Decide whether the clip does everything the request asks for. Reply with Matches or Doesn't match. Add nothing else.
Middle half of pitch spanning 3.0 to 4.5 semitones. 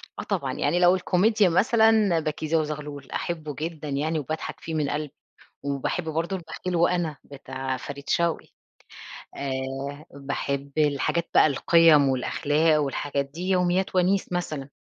Matches